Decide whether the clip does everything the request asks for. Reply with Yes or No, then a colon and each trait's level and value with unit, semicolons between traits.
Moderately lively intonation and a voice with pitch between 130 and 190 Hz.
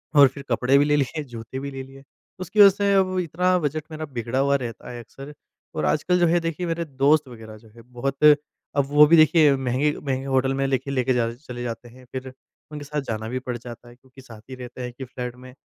Yes: average, 3.3 semitones; low, 135 Hz